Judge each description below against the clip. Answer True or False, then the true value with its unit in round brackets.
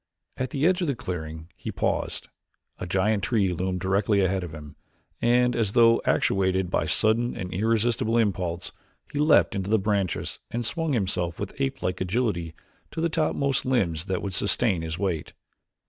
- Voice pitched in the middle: False (100 Hz)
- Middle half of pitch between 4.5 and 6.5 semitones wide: True (4.8 semitones)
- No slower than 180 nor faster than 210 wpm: False (170 wpm)